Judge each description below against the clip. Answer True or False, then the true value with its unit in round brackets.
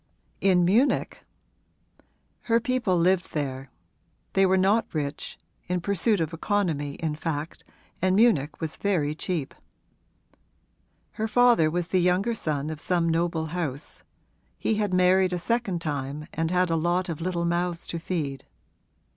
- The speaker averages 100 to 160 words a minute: True (145 wpm)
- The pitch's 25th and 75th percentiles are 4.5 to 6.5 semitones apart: False (3.3 semitones)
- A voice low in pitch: False (175 Hz)